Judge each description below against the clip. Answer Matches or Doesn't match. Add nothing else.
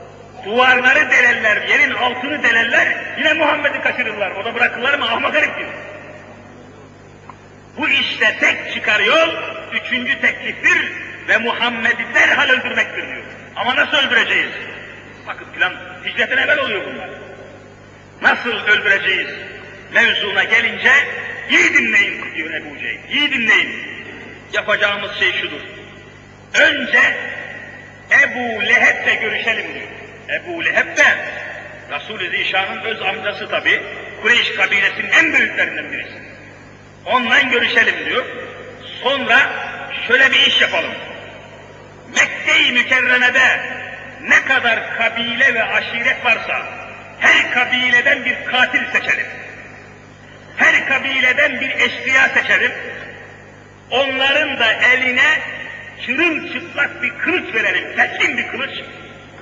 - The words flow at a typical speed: Matches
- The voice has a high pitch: Matches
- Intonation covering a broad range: Doesn't match